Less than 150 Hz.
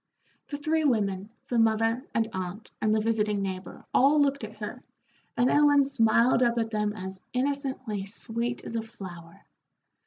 No: high, 225 Hz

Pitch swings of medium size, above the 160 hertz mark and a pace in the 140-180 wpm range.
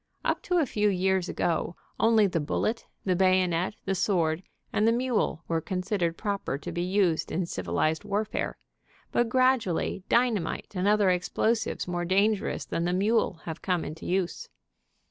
Yes: average, 3.6 semitones; medium, 185 Hz; average, 160 wpm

